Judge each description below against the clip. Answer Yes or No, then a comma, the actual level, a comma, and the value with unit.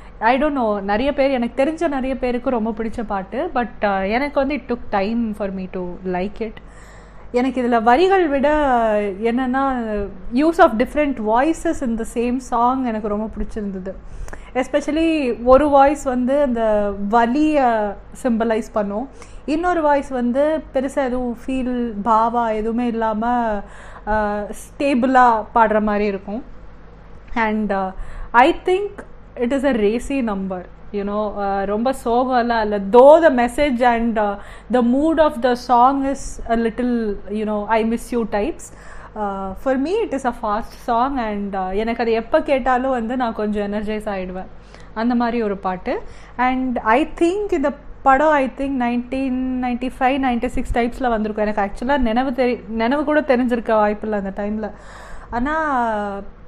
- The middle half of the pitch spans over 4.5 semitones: No, average, 3.8 semitones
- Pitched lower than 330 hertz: Yes, high, 240 Hz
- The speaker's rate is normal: No, fast, 145 wpm